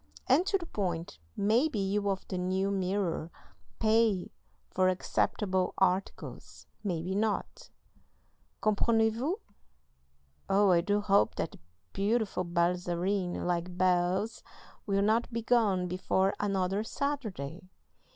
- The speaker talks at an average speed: No, slow, 110 wpm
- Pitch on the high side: Yes, high, 195 Hz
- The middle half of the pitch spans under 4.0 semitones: Yes, average, 3.1 semitones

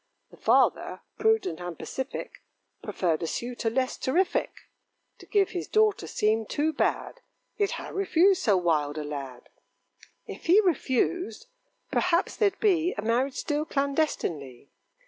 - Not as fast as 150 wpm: Yes, slow, 135 wpm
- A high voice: Yes, very high, 275 Hz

